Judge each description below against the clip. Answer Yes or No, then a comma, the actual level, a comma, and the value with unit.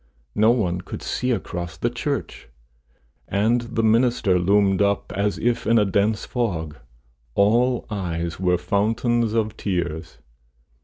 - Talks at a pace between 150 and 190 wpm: No, slow, 135 wpm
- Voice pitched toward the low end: Yes, low, 105 Hz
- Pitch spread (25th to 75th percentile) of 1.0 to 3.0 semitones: No, average, 4.2 semitones